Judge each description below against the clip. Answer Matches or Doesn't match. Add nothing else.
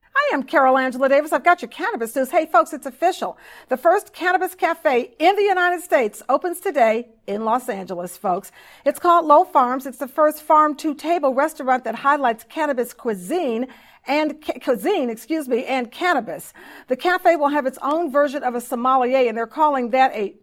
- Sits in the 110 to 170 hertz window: Doesn't match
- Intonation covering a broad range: Doesn't match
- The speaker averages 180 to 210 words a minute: Matches